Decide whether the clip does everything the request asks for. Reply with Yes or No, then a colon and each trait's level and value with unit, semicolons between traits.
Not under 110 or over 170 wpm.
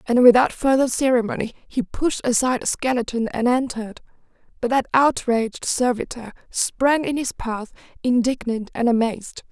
Yes: average, 140 wpm